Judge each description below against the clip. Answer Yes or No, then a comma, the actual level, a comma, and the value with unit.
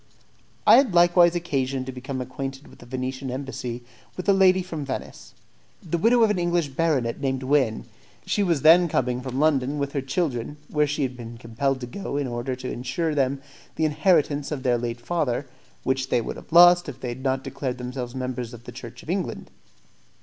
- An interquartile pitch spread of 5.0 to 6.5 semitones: No, average, 4.2 semitones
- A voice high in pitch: No, low, 135 Hz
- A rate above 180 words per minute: Yes, average, 200 wpm